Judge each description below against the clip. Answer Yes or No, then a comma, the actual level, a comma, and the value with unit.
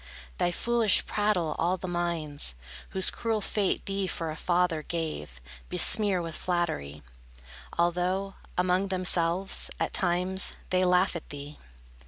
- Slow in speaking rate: Yes, slow, 130 wpm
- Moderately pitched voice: Yes, medium, 180 Hz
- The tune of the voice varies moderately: No, narrow, 2.3 semitones